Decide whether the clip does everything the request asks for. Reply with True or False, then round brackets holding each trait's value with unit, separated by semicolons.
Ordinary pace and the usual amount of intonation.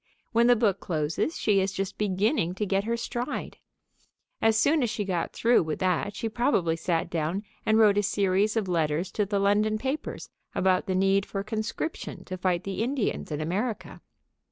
True (185 wpm; 3.2 semitones)